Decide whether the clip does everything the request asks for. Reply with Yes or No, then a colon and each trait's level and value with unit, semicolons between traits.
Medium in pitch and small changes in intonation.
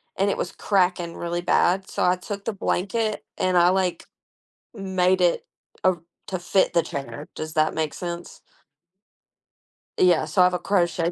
Yes: medium, 180 Hz; narrow, 1.7 semitones